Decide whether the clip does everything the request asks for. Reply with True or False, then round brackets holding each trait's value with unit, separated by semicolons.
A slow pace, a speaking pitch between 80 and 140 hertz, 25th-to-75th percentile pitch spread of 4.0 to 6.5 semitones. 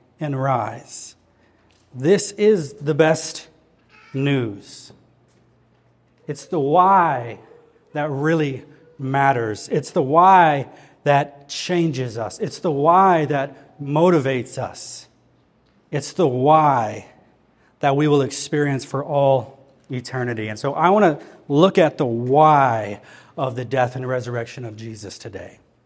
False (120 wpm; 135 Hz; 3.5 semitones)